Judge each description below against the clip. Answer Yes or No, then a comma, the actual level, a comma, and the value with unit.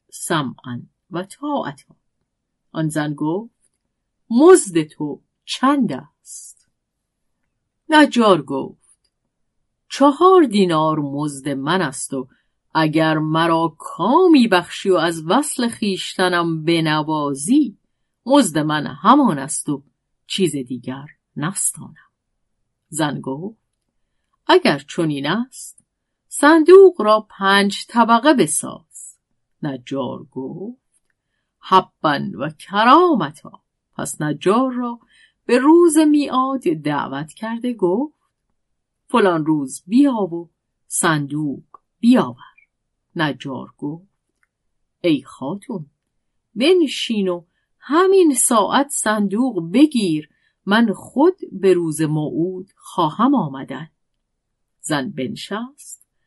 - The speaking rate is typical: No, slow, 90 wpm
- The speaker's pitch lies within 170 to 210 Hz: Yes, medium, 185 Hz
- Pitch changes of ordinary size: No, wide, 8.9 semitones